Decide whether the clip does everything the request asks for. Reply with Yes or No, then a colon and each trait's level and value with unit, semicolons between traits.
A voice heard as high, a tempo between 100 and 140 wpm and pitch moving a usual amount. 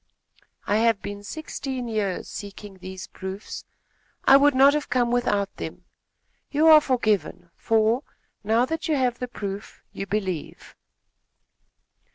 Yes: high, 225 Hz; slow, 135 wpm; average, 4.4 semitones